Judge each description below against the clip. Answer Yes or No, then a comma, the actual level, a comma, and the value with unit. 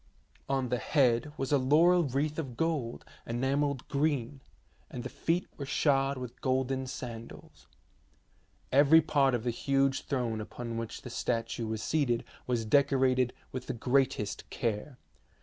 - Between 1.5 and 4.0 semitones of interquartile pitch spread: Yes, average, 2.8 semitones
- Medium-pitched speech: No, low, 130 Hz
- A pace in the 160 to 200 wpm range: No, average, 145 wpm